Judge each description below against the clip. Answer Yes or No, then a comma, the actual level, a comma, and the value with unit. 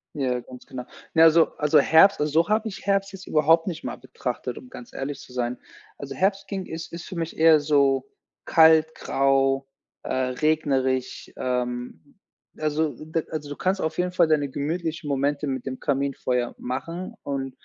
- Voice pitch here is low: No, medium, 150 Hz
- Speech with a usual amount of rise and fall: Yes, average, 3.6 semitones